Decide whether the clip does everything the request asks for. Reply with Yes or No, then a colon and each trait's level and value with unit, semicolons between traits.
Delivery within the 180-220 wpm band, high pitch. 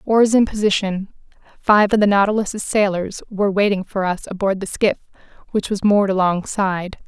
No: average, 160 wpm; high, 200 Hz